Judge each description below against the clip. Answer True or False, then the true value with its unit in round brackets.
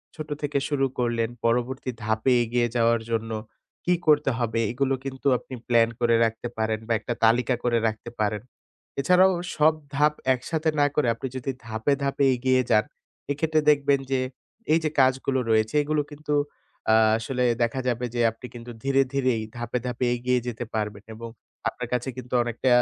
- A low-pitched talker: True (125 Hz)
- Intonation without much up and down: False (3.1 semitones)